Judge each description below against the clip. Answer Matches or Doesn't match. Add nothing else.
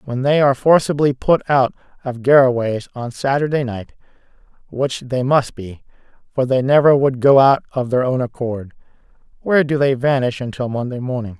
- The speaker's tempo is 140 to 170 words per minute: Matches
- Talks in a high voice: Doesn't match